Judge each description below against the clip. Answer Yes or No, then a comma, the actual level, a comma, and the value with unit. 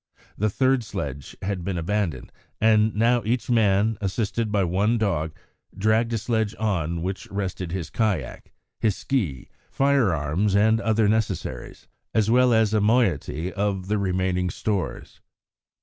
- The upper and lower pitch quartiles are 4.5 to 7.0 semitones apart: No, average, 3.3 semitones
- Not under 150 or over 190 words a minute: No, average, 140 wpm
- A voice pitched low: Yes, low, 105 Hz